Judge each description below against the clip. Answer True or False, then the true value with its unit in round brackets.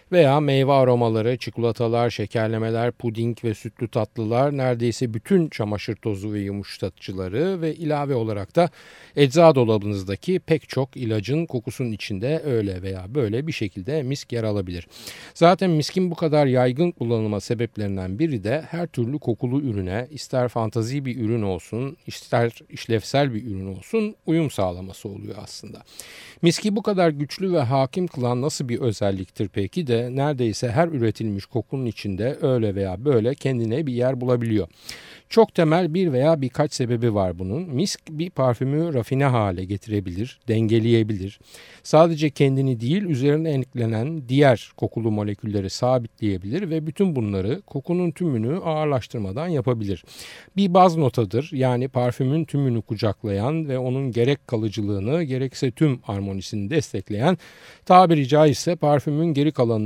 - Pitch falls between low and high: False (125 Hz)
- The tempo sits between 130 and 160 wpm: True (135 wpm)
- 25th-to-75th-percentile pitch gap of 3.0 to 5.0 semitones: False (5.6 semitones)